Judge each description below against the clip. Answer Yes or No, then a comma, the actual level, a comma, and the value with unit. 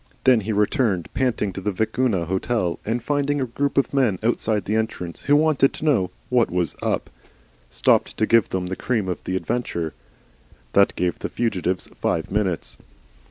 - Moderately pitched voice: No, low, 110 Hz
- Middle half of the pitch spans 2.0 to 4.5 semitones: No, wide, 5.4 semitones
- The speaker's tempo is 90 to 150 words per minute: No, average, 175 wpm